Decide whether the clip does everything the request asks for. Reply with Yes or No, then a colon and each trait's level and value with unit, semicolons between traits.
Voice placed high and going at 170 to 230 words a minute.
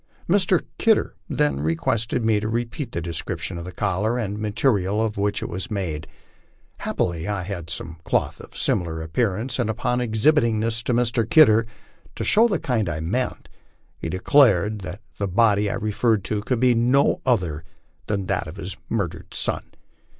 No: low, 105 Hz; average, 180 wpm